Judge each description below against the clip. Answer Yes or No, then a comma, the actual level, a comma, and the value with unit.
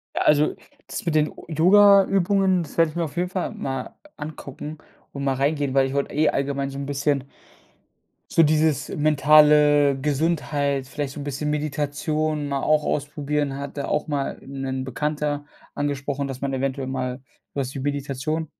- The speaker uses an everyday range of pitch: No, narrow, 1.8 semitones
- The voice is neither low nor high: Yes, medium, 145 Hz